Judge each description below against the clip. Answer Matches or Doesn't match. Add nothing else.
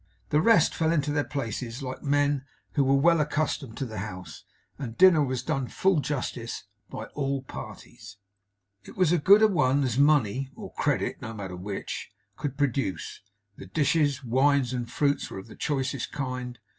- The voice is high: Doesn't match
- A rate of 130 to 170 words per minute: Doesn't match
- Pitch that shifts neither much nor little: Matches